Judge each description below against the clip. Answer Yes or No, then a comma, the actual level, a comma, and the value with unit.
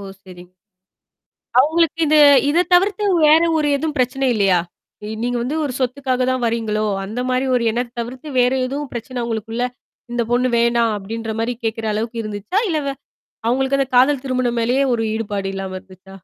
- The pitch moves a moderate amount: Yes, average, 3.3 semitones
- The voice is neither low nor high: No, high, 245 Hz